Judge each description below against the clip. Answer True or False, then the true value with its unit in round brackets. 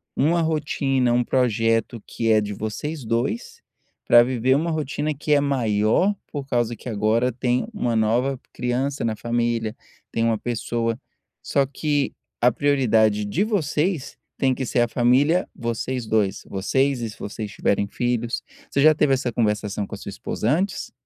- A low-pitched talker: True (120 Hz)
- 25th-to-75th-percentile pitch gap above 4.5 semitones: False (3.9 semitones)